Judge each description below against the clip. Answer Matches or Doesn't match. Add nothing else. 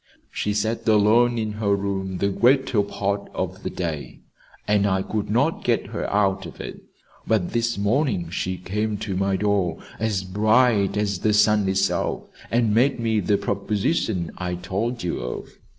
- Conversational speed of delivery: Matches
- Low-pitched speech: Matches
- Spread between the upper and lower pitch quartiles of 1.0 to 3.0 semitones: Matches